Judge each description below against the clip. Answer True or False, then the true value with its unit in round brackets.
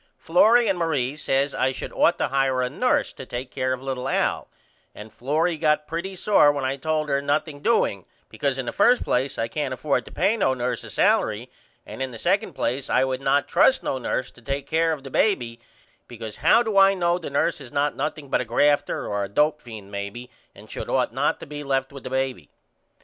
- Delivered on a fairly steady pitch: False (3.7 semitones)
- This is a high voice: False (140 Hz)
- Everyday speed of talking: False (225 wpm)